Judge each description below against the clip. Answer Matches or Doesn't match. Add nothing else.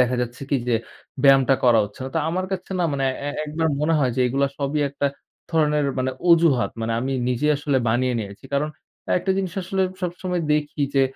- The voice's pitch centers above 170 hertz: Doesn't match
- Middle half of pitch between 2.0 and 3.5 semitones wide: Doesn't match